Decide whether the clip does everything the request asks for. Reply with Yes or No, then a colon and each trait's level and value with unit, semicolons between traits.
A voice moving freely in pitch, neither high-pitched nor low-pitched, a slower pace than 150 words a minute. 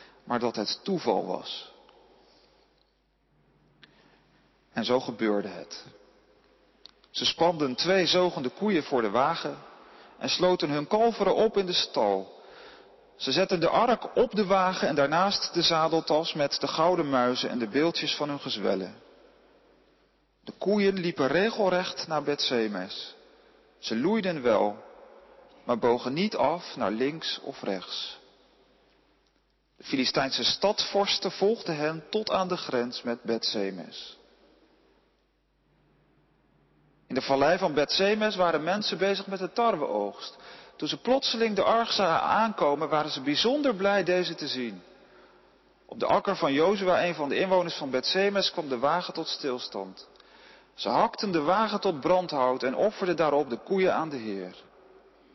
Yes: wide, 5.9 semitones; medium, 180 Hz; average, 140 wpm